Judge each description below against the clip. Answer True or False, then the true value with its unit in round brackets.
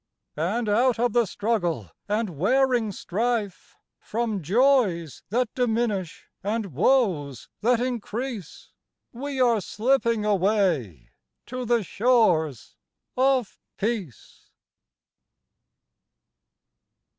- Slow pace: True (85 wpm)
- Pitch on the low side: False (220 Hz)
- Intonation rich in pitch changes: False (4.8 semitones)